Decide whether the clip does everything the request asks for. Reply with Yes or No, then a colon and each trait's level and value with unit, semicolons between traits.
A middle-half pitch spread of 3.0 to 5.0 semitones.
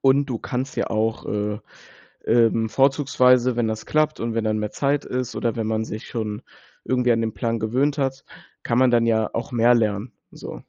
No: narrow, 2.6 semitones